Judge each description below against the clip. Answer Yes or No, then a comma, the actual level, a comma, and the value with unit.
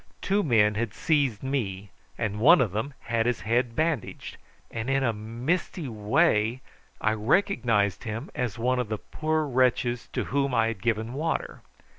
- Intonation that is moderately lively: Yes, average, 3.9 semitones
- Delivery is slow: No, average, 165 wpm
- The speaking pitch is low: Yes, low, 120 Hz